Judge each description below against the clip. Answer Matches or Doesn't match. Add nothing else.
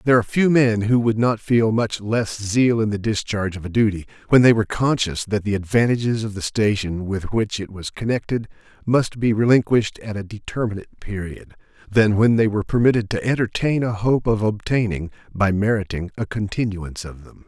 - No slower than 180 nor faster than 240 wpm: Matches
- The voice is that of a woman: Doesn't match